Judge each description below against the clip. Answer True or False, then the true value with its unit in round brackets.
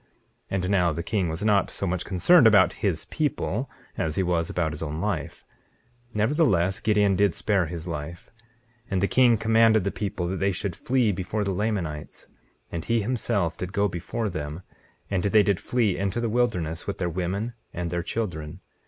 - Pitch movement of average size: True (3.7 semitones)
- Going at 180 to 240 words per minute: True (190 wpm)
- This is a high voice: False (95 Hz)